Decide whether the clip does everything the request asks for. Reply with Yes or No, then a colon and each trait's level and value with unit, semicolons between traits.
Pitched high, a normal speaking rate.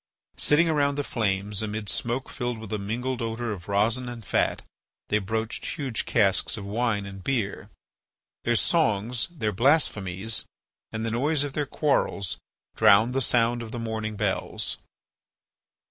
No: low, 115 Hz; average, 150 wpm